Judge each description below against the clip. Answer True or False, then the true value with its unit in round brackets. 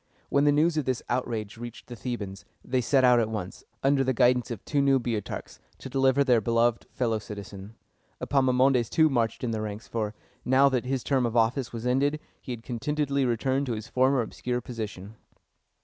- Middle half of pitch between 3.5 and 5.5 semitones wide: False (3.0 semitones)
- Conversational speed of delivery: True (195 wpm)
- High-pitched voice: False (125 Hz)